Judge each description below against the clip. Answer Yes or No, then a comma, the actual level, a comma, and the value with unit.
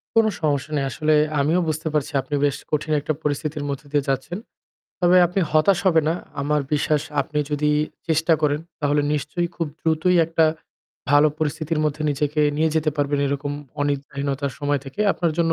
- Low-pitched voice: No, medium, 150 Hz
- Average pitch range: No, narrow, 1.8 semitones